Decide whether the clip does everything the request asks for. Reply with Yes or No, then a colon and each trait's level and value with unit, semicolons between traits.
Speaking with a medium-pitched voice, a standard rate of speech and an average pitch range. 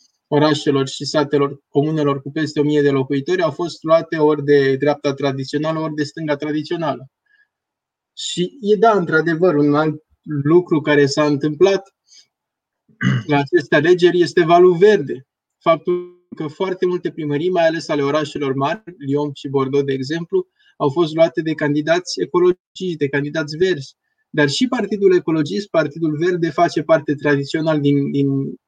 Yes: medium, 155 Hz; average, 150 wpm; average, 3.5 semitones